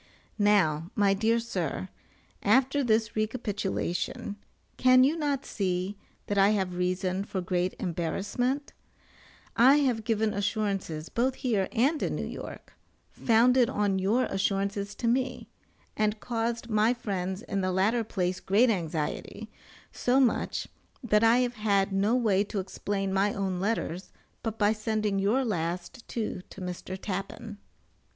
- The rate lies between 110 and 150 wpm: Yes, average, 140 wpm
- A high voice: Yes, high, 205 Hz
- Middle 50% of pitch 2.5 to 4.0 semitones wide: Yes, average, 3.4 semitones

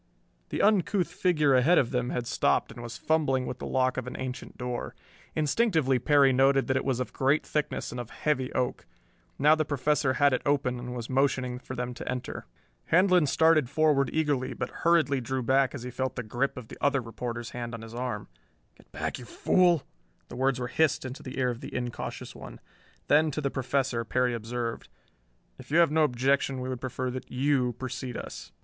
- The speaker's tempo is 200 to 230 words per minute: Yes, fast, 205 wpm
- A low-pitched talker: Yes, low, 130 Hz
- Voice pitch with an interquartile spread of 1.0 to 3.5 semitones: Yes, average, 2.9 semitones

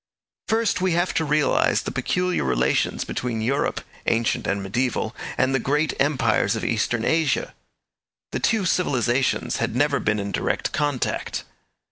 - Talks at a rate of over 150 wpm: No, average, 145 wpm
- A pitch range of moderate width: No, wide, 5.8 semitones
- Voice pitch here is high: No, low, 135 Hz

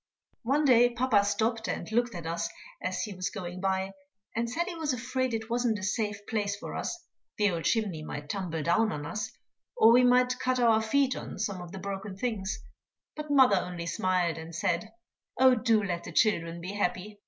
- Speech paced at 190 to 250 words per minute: Yes, average, 200 wpm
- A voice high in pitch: Yes, high, 210 Hz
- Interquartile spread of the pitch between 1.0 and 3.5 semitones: No, average, 4.7 semitones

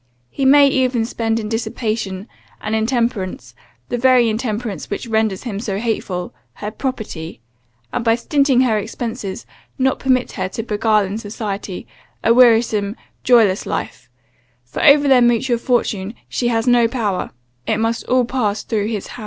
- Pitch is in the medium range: No, high, 225 Hz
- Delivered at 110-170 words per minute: Yes, average, 155 wpm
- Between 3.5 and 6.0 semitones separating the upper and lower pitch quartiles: No, average, 2.8 semitones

